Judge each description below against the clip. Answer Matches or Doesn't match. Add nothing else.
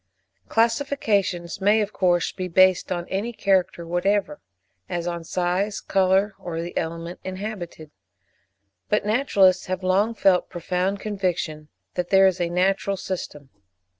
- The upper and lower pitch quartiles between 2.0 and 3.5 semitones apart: Matches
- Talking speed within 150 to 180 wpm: Doesn't match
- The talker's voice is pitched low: Doesn't match